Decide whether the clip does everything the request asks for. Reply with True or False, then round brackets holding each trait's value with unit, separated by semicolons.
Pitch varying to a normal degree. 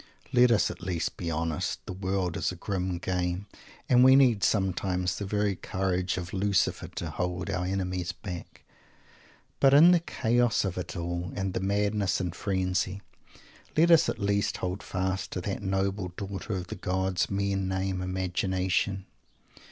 False (1.8 semitones)